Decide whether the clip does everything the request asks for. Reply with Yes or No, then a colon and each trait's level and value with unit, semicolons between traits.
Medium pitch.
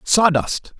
Yes: medium, 165 Hz